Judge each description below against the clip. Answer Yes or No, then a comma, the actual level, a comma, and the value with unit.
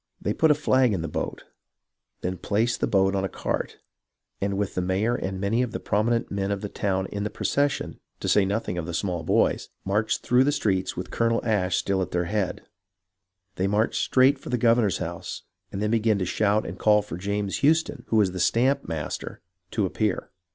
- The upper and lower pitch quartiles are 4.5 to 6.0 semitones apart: No, average, 3.5 semitones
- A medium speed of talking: No, fast, 210 wpm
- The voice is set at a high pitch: No, low, 105 Hz